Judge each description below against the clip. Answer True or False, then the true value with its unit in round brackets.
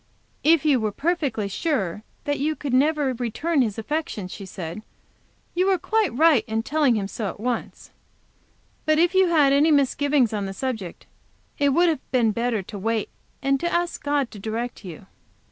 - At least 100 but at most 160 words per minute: False (180 wpm)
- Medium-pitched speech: False (265 Hz)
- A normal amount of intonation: False (6.1 semitones)